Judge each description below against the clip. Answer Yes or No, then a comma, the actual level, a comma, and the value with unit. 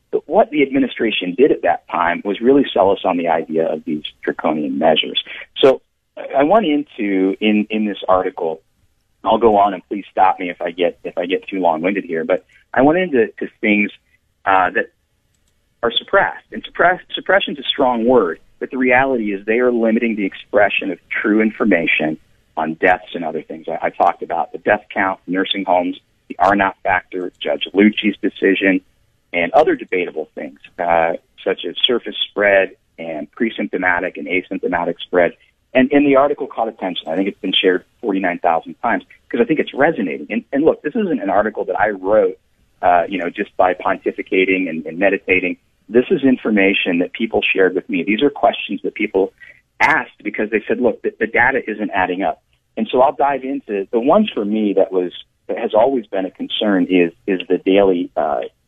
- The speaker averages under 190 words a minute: No, average, 195 wpm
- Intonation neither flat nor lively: No, wide, 5.9 semitones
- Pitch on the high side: No, low, 105 Hz